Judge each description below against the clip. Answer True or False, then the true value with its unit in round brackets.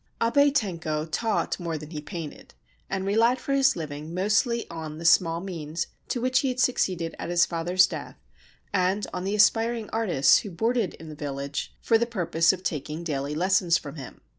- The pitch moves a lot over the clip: True (6.0 semitones)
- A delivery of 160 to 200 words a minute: True (190 wpm)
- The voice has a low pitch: False (180 Hz)